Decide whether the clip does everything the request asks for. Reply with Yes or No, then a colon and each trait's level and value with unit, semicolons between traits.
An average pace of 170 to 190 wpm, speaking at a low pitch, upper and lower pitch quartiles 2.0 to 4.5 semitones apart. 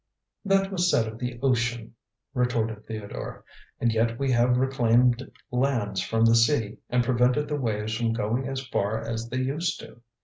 Yes: average, 175 wpm; low, 120 Hz; narrow, 2.6 semitones